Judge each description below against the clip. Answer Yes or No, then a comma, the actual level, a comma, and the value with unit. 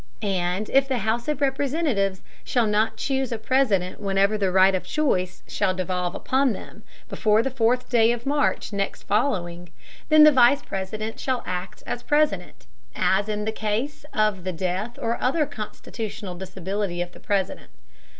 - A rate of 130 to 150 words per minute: No, average, 165 wpm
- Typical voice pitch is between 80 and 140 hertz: No, high, 215 Hz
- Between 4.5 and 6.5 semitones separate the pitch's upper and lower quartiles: Yes, average, 5.3 semitones